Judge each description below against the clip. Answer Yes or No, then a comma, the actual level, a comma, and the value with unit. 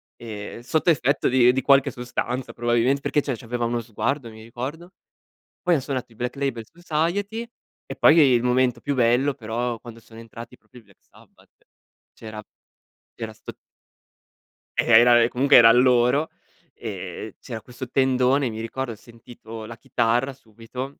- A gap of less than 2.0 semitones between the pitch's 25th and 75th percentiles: No, average, 2.8 semitones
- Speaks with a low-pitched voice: Yes, low, 125 Hz